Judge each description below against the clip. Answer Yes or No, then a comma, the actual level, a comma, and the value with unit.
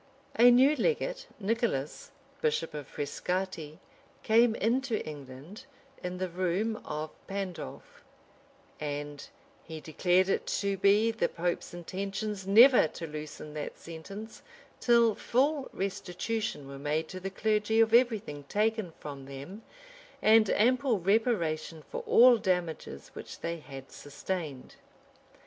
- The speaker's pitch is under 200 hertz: Yes, high, 190 Hz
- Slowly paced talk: Yes, slow, 125 wpm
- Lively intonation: Yes, wide, 6.3 semitones